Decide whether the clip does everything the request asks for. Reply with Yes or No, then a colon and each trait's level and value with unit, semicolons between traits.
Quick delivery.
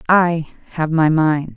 No: average, 155 wpm